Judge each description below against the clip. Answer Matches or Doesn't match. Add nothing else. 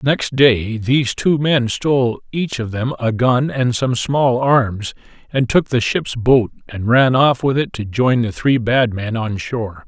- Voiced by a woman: Doesn't match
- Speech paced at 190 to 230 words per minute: Matches